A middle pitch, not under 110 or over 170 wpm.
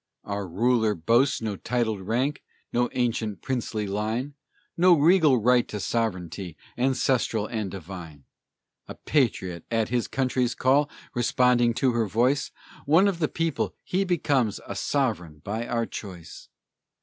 No: low, 120 Hz; slow, 135 wpm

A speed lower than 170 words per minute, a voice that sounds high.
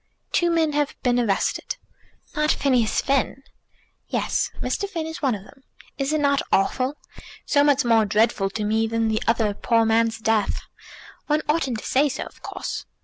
No: average, 175 wpm; very high, 250 Hz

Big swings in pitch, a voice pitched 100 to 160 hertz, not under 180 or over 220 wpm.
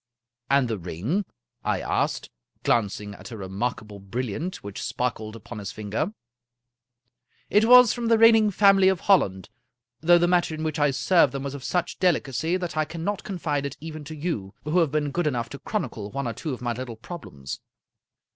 Yes: wide, 7.2 semitones; medium, 140 Hz; average, 200 wpm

